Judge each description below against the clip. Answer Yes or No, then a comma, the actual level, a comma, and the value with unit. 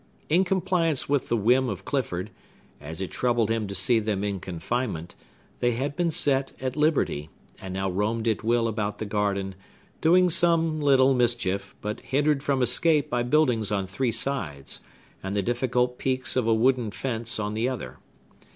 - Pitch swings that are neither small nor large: Yes, average, 4.9 semitones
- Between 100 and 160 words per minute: No, average, 175 wpm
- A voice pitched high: No, low, 120 Hz